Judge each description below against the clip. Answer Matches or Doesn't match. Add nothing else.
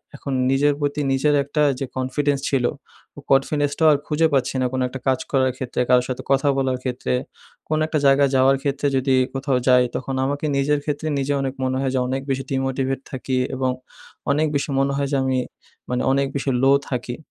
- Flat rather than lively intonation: Matches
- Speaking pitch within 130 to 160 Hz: Matches